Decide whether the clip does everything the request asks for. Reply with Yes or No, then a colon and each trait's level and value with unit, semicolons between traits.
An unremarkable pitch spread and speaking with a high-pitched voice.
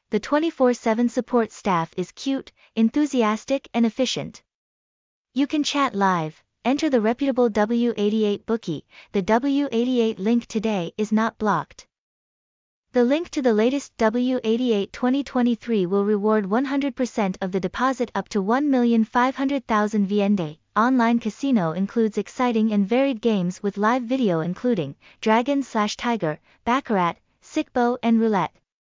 Yes: average, 3.4 semitones; high, 230 Hz